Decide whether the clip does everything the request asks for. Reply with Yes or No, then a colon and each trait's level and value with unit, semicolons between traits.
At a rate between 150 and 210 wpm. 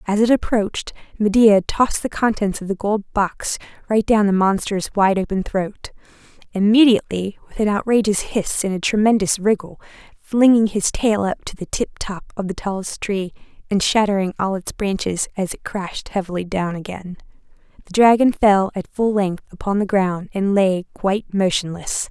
Yes: average, 165 wpm